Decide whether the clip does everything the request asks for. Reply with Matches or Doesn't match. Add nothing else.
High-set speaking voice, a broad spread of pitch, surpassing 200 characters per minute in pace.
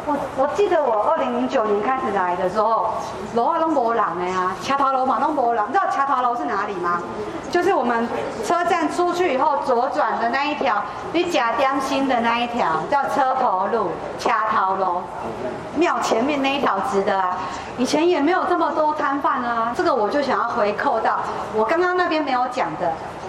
Matches